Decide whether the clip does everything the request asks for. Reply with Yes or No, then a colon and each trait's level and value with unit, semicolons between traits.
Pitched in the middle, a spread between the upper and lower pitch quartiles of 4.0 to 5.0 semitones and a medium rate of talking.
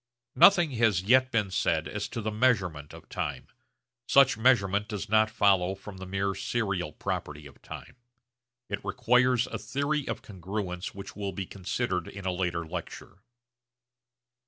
No: low, 100 Hz; average, 4.4 semitones; average, 155 wpm